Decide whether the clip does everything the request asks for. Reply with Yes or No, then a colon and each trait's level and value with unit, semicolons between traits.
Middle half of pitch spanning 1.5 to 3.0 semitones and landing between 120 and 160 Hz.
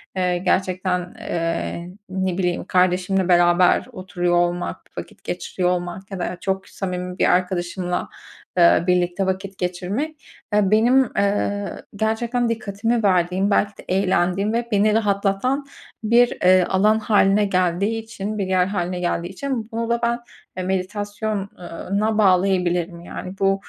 No: narrow, 2.6 semitones; high, 190 Hz